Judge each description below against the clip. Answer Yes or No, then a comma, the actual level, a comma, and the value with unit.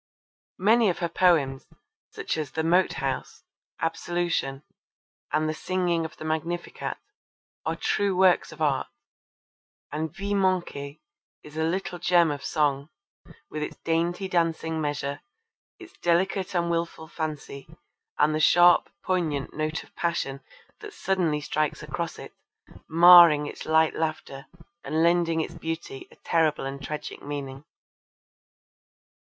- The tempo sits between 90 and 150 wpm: Yes, slow, 135 wpm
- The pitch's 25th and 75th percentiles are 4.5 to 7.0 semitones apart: No, narrow, 2.6 semitones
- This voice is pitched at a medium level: Yes, medium, 160 Hz